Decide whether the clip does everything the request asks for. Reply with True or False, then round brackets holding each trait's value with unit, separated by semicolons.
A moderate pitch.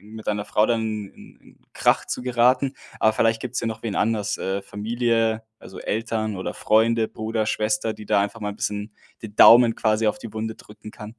False (110 Hz)